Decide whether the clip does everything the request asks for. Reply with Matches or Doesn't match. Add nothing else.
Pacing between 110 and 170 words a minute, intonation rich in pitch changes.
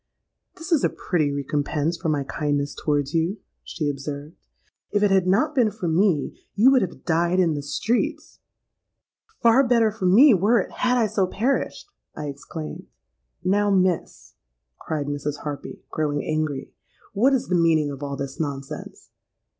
Matches